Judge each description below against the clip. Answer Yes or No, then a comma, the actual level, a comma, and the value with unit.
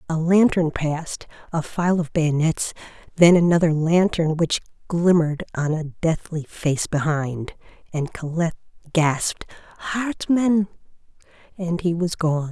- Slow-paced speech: Yes, slow, 120 wpm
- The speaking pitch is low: No, medium, 165 Hz